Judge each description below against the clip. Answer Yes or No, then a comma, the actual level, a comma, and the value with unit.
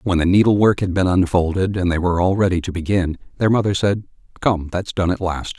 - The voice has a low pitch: Yes, very low, 90 Hz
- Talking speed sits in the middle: No, fast, 235 wpm